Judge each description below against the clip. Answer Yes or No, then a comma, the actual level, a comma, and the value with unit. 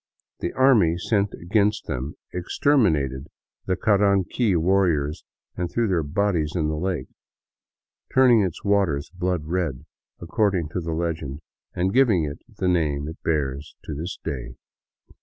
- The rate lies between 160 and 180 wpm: No, average, 140 wpm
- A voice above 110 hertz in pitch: No, very low, 85 Hz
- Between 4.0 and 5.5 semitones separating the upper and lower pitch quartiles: Yes, average, 4.6 semitones